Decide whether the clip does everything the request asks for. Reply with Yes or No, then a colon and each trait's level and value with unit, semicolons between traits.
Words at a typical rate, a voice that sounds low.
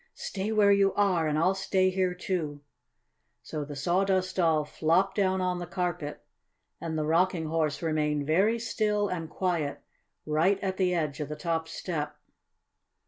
No: average, 160 wpm; medium, 175 Hz